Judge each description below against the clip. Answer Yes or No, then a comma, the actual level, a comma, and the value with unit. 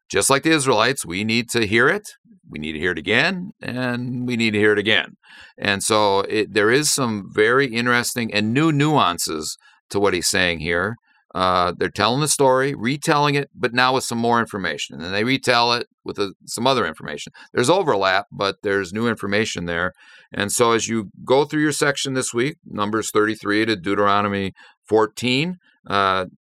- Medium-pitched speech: No, low, 115 Hz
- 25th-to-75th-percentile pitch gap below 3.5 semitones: No, average, 4.5 semitones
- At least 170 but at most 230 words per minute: Yes, average, 190 wpm